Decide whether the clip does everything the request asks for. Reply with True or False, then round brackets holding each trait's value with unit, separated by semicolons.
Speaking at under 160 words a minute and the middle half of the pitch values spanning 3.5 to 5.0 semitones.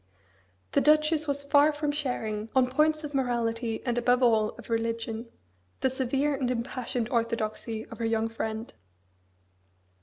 True (145 wpm; 3.8 semitones)